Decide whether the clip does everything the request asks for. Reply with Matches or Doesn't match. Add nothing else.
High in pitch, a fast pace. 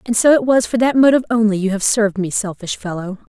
Matches